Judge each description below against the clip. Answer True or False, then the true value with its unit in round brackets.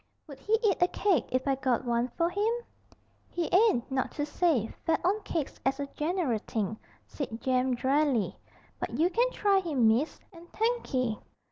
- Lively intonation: True (6.2 semitones)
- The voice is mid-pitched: False (295 Hz)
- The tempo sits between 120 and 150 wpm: False (175 wpm)